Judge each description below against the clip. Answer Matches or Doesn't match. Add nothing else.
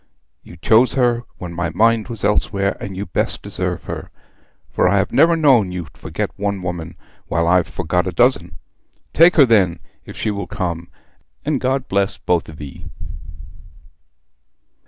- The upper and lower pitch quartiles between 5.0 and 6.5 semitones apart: Matches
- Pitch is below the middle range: Matches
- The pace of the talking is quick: Doesn't match